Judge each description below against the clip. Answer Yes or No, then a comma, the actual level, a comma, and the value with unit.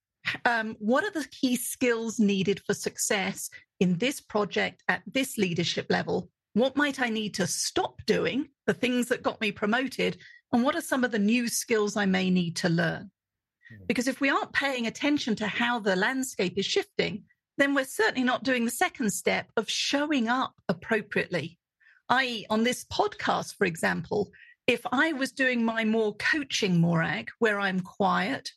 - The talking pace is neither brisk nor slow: Yes, average, 175 wpm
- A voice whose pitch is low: No, high, 235 Hz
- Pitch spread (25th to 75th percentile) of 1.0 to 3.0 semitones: No, average, 4.4 semitones